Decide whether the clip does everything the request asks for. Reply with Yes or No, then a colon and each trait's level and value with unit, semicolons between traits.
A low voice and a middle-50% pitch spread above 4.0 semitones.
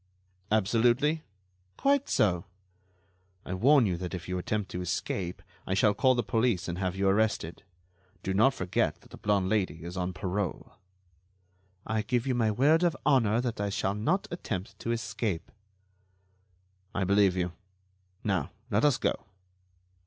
Yes: low, 105 Hz; average, 4.4 semitones